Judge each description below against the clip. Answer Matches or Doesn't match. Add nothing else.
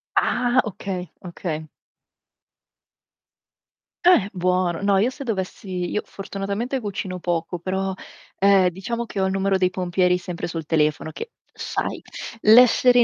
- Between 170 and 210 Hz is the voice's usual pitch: Matches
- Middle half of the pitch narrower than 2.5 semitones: Doesn't match